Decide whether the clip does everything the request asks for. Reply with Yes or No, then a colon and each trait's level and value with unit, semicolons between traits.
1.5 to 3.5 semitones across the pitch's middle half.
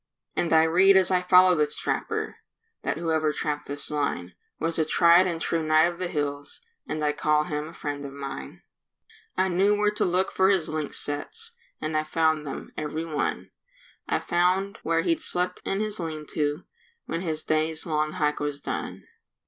Yes: average, 3.2 semitones